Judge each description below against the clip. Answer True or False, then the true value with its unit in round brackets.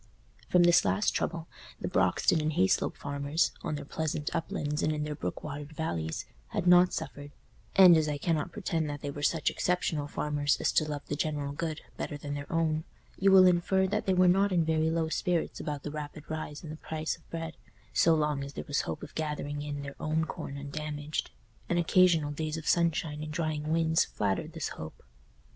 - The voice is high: False (155 Hz)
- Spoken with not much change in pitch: True (2.2 semitones)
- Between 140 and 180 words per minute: False (205 wpm)